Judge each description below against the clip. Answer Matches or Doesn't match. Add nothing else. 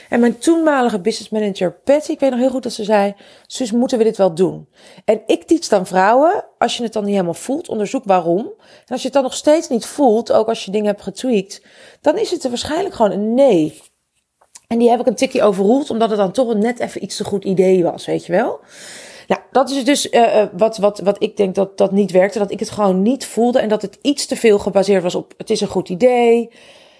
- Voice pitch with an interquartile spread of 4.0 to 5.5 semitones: Matches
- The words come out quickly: Matches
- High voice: Matches